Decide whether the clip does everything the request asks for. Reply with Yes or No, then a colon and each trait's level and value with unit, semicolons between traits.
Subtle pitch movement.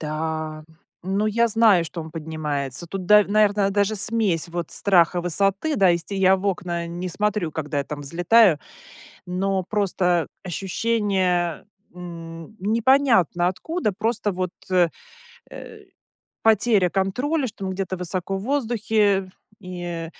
No: average, 3.6 semitones